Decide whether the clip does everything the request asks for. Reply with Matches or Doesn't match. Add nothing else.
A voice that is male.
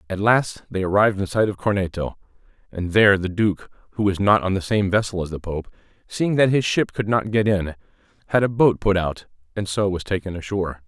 Matches